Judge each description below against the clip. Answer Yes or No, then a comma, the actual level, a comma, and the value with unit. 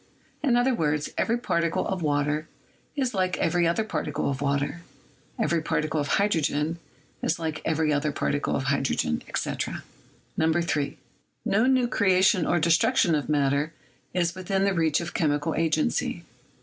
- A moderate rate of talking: Yes, average, 150 wpm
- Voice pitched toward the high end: No, medium, 160 Hz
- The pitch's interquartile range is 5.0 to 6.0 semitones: No, average, 3.8 semitones